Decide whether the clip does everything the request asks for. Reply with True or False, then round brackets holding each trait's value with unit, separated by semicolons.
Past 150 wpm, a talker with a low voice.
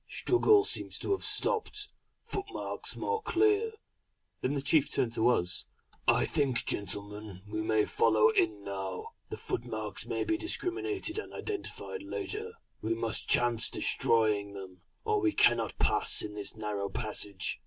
False (145 wpm; 120 Hz)